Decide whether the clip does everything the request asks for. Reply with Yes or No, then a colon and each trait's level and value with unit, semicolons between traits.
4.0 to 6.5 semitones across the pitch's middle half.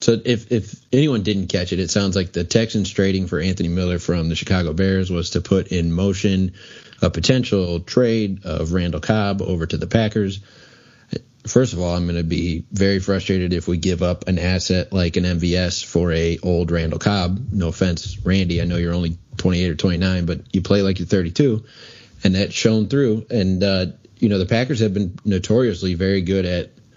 No: average, 3.3 semitones